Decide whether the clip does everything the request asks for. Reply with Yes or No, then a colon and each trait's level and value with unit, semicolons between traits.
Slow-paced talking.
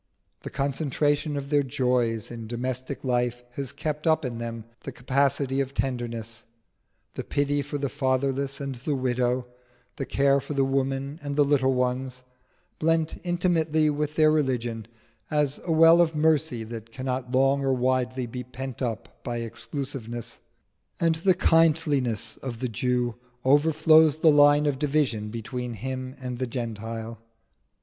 No: average, 150 wpm